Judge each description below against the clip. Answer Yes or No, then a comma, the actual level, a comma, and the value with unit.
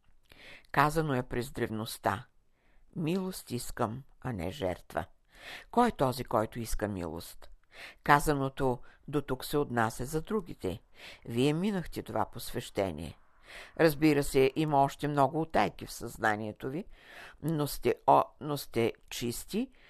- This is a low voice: Yes, low, 130 Hz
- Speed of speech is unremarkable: Yes, average, 125 wpm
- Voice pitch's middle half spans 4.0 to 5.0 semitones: Yes, average, 4.6 semitones